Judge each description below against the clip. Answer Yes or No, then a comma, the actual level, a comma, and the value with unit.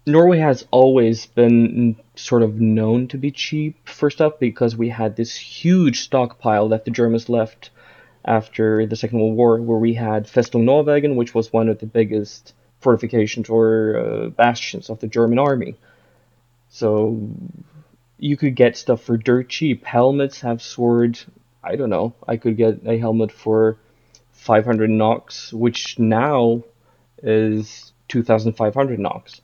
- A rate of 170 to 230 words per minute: No, average, 150 wpm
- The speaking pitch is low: Yes, low, 115 Hz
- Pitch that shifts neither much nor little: No, narrow, 1.8 semitones